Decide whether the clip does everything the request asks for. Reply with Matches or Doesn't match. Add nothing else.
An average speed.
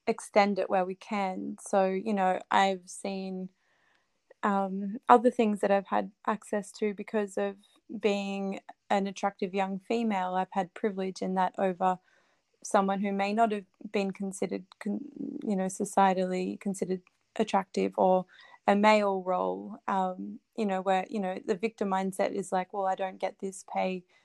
Matches